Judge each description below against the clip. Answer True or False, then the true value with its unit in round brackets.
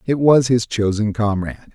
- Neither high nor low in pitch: False (115 Hz)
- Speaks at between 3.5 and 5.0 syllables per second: True (4.9 syllables/s)